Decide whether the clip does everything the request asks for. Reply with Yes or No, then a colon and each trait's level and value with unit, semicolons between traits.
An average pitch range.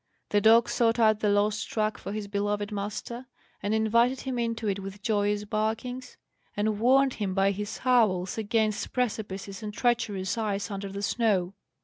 No: narrow, 2.2 semitones